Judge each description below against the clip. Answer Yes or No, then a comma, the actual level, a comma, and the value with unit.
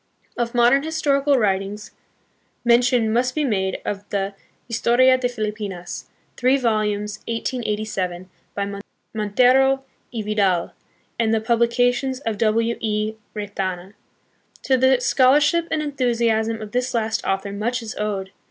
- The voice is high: Yes, high, 225 Hz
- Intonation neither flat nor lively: Yes, average, 3.3 semitones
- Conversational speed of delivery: No, slow, 125 wpm